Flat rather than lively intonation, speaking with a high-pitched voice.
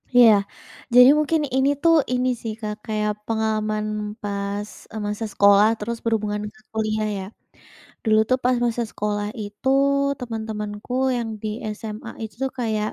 Yes: narrow, 1.9 semitones; high, 215 Hz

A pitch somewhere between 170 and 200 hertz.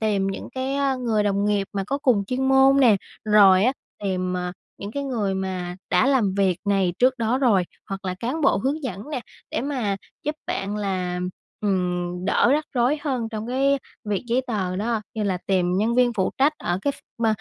No: high, 210 Hz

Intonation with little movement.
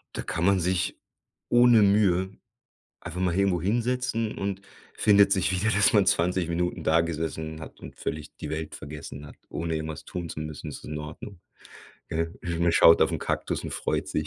No: average, 3.9 semitones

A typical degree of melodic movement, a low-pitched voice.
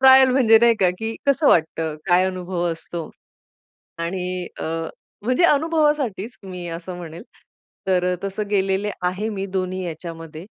No: average, 4.3 semitones; medium, 185 Hz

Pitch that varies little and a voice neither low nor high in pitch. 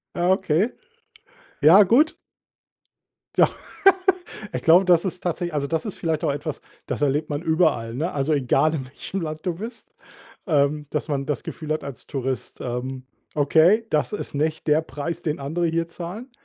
No: average, 3.3 semitones; medium, 155 Hz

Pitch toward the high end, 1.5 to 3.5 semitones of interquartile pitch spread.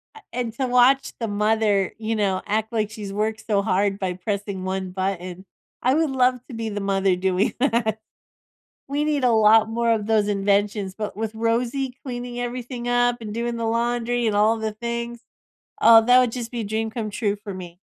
Yes: high, 220 Hz; average, 2.9 semitones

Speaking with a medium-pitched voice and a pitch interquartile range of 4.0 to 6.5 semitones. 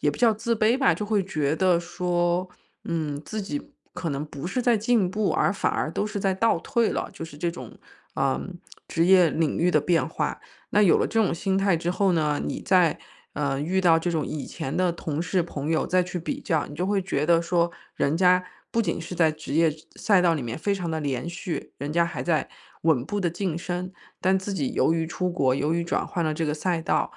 No: medium, 175 Hz; average, 3.4 semitones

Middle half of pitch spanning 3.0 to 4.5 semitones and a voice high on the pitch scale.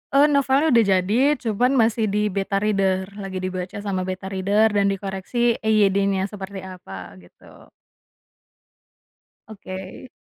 No: narrow, 2.5 semitones; high, 195 Hz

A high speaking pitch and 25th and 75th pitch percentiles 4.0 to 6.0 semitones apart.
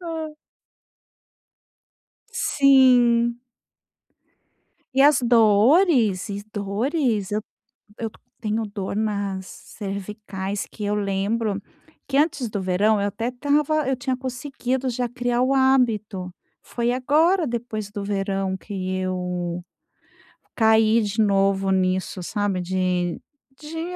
Yes: high, 215 Hz; average, 4.5 semitones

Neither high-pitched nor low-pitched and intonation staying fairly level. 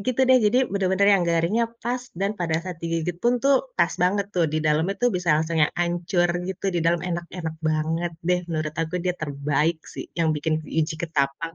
No: medium, 170 Hz; average, 3.1 semitones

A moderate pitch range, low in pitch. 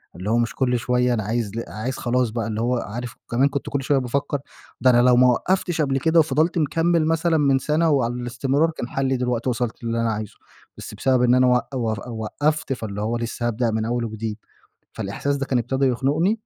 Yes: average, 3.3 semitones; low, 125 Hz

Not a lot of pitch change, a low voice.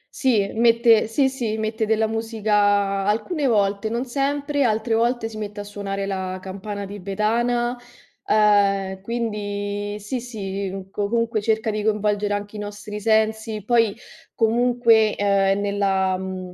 No: narrow, 2.2 semitones; high, 215 Hz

